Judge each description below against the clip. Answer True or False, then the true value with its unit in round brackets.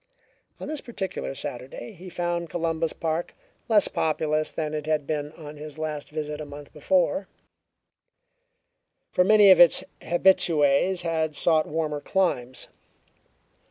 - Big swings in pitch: False (2.7 semitones)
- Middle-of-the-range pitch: True (160 Hz)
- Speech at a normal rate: False (130 wpm)